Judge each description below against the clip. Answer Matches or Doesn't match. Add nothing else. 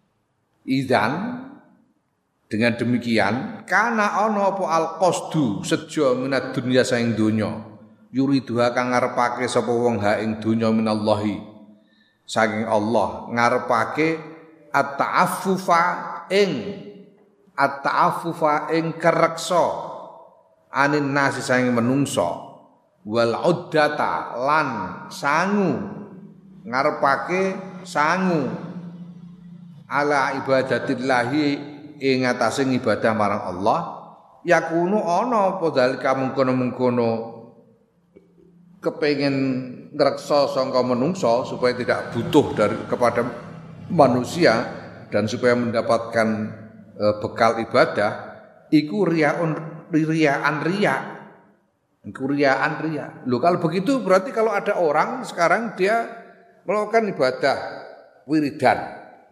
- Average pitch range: Doesn't match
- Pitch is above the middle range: Doesn't match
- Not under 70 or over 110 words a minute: Matches